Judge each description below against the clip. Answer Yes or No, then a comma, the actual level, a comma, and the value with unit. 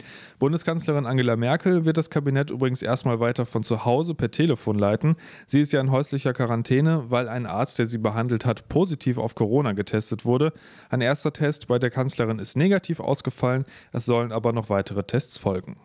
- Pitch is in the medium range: No, low, 125 Hz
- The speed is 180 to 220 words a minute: Yes, average, 185 wpm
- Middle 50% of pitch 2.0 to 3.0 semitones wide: No, average, 3.8 semitones